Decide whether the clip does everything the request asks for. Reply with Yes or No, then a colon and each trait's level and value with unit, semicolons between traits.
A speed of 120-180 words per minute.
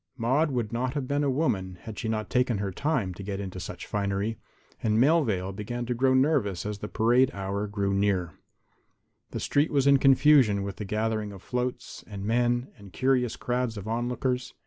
No: average, 190 wpm